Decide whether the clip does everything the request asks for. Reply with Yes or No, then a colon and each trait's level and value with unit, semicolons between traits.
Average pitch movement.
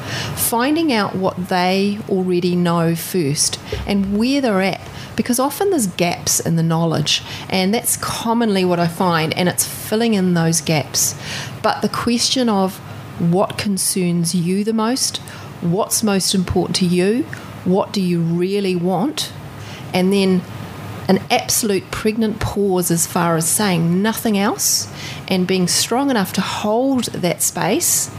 Yes: average, 4.1 semitones